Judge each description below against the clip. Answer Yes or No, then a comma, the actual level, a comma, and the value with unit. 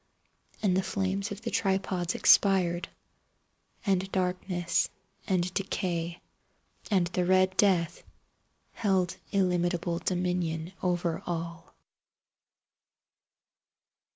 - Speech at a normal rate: No, slow, 85 wpm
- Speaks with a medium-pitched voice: Yes, medium, 180 Hz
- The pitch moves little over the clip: Yes, narrow, 1.7 semitones